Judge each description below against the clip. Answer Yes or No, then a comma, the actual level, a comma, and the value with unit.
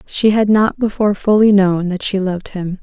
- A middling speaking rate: No, fast, 215 wpm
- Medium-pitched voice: No, high, 200 Hz